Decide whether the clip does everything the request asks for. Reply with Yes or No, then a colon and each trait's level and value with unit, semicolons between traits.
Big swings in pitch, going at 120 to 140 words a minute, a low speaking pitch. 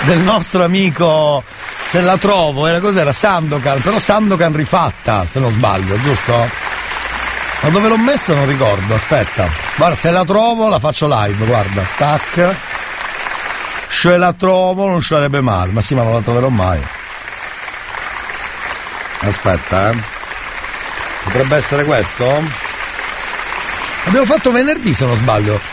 No: wide, 8.3 semitones; average, 130 wpm; medium, 150 Hz